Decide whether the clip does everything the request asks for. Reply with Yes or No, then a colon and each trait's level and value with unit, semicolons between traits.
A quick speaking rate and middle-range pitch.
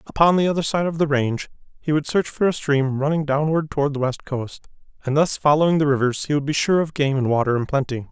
Yes: fast, 250 wpm; medium, 145 Hz